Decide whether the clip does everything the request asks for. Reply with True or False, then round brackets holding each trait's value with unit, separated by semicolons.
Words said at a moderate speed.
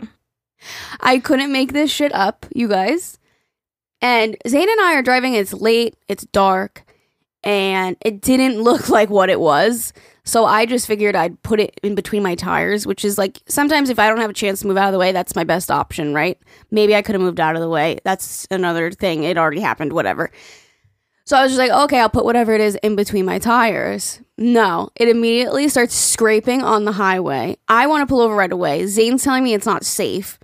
False (215 wpm)